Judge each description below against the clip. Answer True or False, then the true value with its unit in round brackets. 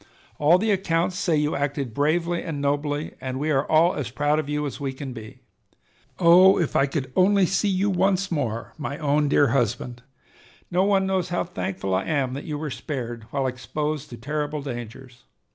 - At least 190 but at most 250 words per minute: True (195 wpm)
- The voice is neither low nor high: True (150 Hz)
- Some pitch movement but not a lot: True (4.5 semitones)